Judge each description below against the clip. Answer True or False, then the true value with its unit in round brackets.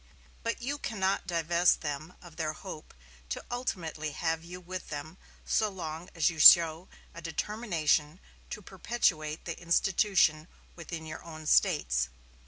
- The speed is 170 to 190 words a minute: False (140 wpm)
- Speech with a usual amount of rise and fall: True (3.1 semitones)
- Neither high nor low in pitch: True (165 Hz)